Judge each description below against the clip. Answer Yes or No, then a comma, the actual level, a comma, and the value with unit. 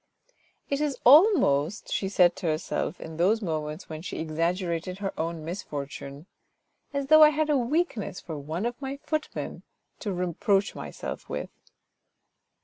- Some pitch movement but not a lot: No, wide, 8.5 semitones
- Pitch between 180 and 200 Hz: Yes, medium, 185 Hz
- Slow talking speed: No, average, 155 wpm